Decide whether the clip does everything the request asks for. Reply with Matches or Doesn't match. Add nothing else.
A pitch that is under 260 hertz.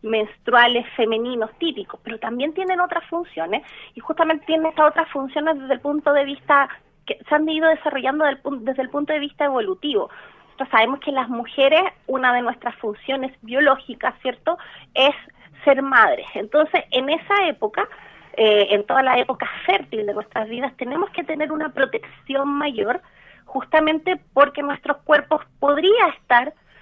Doesn't match